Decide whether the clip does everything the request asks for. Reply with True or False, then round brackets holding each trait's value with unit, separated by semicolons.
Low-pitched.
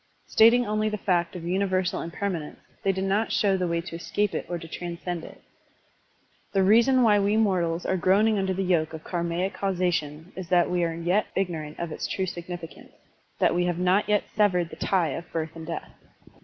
False (180 Hz)